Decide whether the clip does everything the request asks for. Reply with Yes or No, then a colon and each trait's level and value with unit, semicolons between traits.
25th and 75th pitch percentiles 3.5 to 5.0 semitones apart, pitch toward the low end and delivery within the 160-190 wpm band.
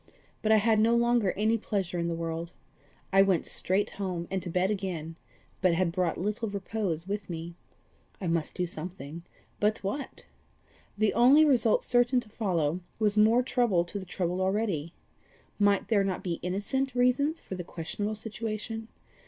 No: average, 4.0 semitones; high, 200 Hz; average, 170 wpm